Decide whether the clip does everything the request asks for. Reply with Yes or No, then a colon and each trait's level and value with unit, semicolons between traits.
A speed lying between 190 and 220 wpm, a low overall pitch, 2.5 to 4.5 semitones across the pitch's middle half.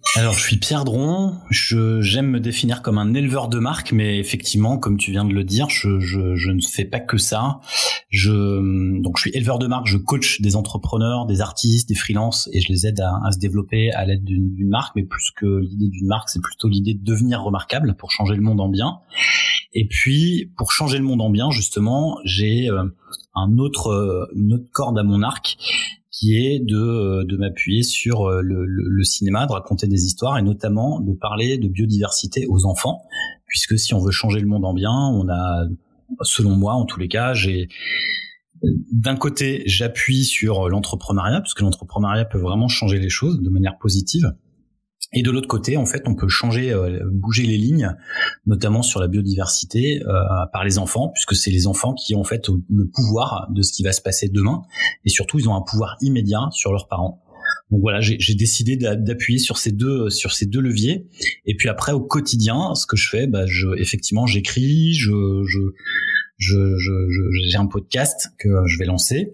Yes: average, 205 wpm; low, 105 Hz; average, 4.1 semitones